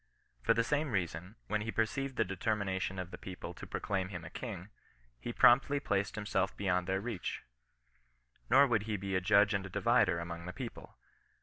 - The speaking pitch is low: Yes, low, 100 Hz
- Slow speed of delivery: No, average, 200 wpm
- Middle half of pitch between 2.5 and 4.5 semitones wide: Yes, average, 3.5 semitones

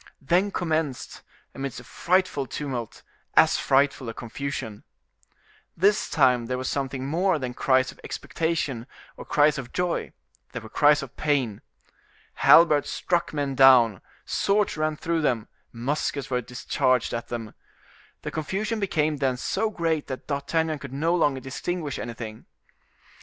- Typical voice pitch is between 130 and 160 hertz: Yes, medium, 140 Hz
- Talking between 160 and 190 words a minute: No, average, 140 wpm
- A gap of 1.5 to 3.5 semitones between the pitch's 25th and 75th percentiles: No, average, 4.2 semitones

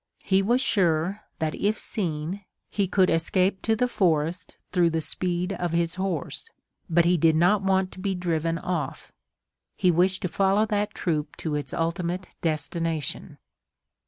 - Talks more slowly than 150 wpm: No, average, 160 wpm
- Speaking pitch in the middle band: Yes, medium, 180 Hz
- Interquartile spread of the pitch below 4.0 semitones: Yes, average, 2.8 semitones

